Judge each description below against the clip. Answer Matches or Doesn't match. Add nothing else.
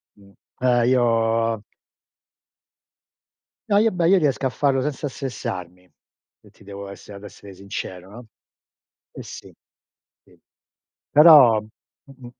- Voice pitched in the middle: Doesn't match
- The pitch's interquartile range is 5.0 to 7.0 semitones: Matches